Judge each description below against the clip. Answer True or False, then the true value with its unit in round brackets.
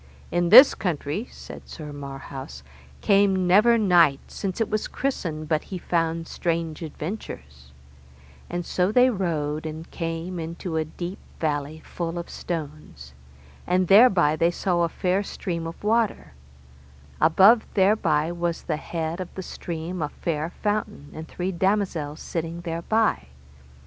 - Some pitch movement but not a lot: True (3.4 semitones)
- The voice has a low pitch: False (170 Hz)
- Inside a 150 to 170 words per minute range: False (140 wpm)